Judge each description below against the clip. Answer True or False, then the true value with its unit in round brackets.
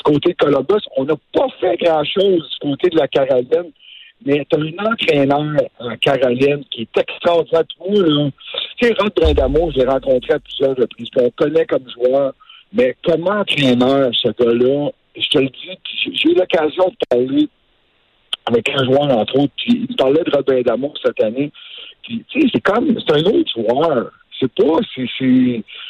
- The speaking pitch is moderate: True (175 Hz)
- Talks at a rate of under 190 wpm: True (175 wpm)